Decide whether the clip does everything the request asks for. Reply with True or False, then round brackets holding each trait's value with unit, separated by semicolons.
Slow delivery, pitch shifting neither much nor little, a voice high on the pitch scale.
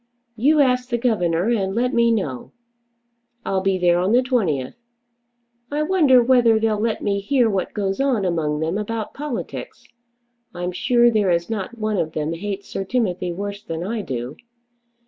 False (170 wpm; 5.0 semitones; 205 Hz)